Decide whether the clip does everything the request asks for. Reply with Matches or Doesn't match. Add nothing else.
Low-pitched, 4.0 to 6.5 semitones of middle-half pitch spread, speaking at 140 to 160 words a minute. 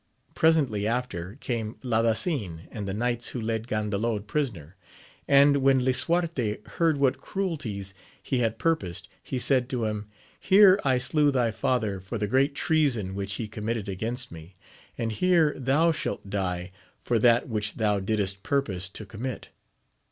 Matches